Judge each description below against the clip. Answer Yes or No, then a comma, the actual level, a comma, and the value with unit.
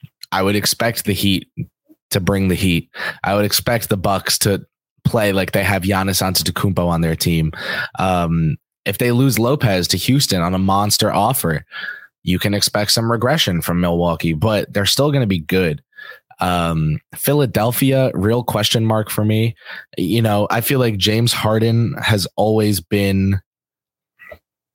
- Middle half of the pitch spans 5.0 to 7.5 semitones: No, average, 4.2 semitones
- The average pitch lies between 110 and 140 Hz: No, low, 100 Hz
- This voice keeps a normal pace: Yes, average, 160 wpm